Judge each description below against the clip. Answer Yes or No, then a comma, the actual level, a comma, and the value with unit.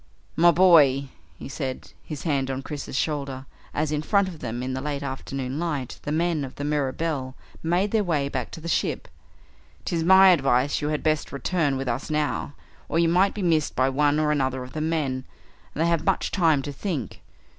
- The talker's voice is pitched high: No, medium, 150 Hz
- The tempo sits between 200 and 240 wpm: Yes, fast, 205 wpm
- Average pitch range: Yes, average, 3.6 semitones